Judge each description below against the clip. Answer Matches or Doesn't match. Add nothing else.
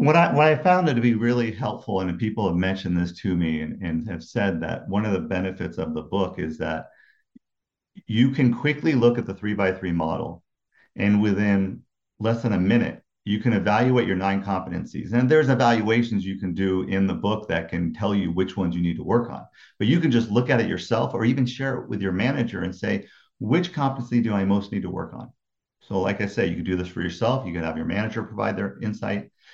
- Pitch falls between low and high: Doesn't match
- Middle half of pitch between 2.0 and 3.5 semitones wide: Doesn't match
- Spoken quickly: Matches